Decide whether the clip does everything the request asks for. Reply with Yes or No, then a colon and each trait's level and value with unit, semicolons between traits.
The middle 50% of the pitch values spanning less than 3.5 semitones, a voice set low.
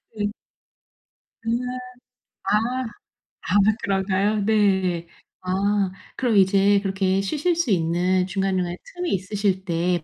No: narrow, 2.5 semitones; high, 195 Hz